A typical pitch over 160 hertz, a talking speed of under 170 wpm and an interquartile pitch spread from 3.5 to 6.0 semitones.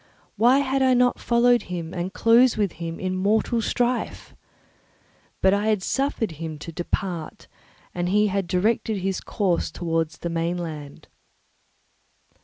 Yes: high, 190 Hz; average, 140 wpm; average, 5.2 semitones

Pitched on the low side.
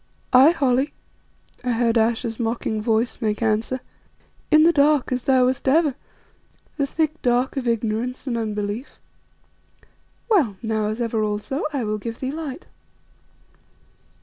No: high, 245 Hz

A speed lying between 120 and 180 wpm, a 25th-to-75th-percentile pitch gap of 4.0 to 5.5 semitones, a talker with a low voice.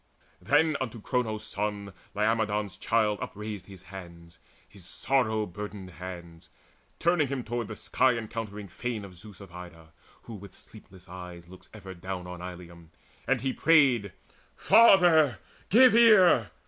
Yes: average, 140 wpm; average, 5.1 semitones; low, 105 Hz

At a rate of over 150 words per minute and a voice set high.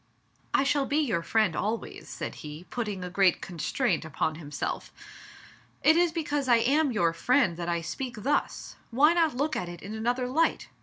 Yes: average, 185 wpm; high, 230 Hz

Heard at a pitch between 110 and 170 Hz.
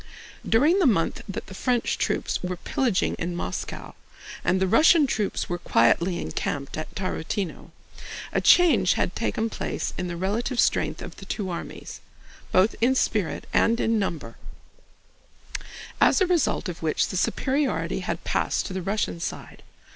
No: high, 195 Hz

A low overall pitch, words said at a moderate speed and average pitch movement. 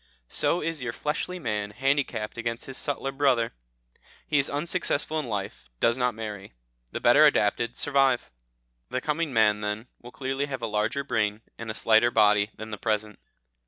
Yes: low, 120 Hz; average, 170 wpm; average, 4.7 semitones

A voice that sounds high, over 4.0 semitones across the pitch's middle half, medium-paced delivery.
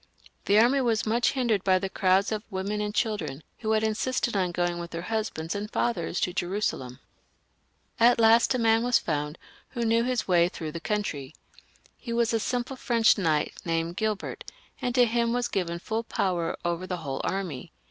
Yes: high, 210 Hz; average, 5.1 semitones; average, 190 wpm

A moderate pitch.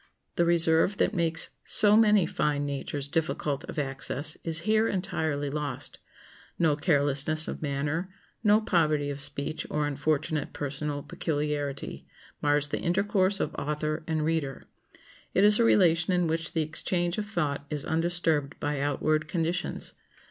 Yes: medium, 155 Hz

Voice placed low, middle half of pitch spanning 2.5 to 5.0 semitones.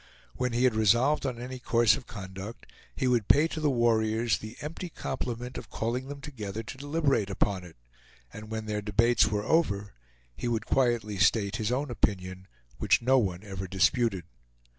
Yes: low, 115 Hz; average, 3.6 semitones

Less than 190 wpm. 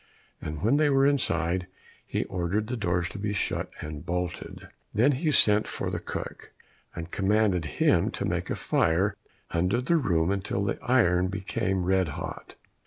Yes: average, 170 wpm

